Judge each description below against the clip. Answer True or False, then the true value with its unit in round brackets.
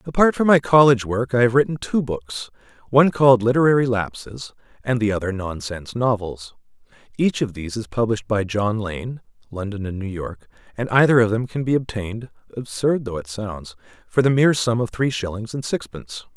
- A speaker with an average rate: True (185 wpm)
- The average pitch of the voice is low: True (115 Hz)